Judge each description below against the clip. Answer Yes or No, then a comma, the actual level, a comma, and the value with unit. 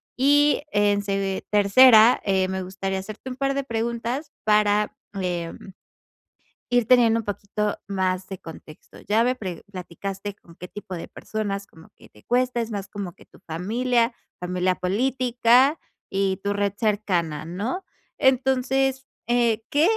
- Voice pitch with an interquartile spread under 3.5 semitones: No, average, 4.5 semitones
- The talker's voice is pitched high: Yes, high, 210 Hz